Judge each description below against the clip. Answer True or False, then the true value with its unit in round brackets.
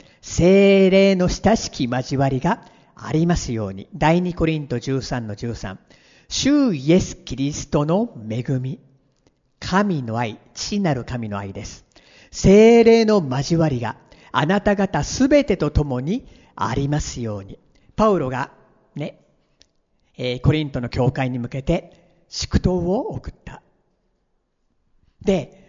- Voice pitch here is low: False (150 Hz)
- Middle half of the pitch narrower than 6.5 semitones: False (7.2 semitones)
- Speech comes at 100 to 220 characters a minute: True (215 characters per minute)